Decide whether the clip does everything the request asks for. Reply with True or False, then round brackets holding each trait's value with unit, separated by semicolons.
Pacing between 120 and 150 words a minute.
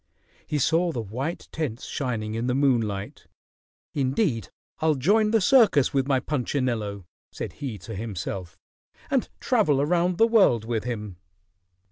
True (140 wpm)